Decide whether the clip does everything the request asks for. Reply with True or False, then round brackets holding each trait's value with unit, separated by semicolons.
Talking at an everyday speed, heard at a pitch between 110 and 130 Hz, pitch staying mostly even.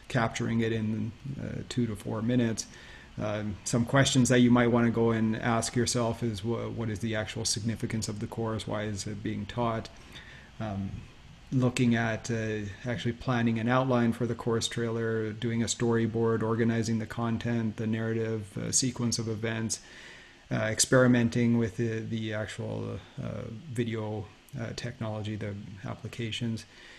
True (160 wpm; 115 Hz; 1.4 semitones)